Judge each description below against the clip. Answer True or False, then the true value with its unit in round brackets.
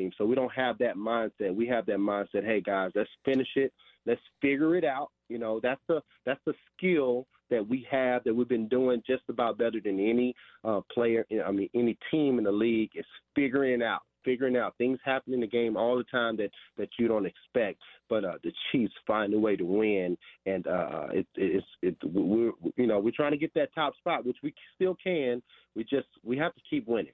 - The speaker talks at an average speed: False (220 wpm)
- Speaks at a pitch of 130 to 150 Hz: False (120 Hz)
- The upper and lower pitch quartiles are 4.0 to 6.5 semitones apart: False (2.9 semitones)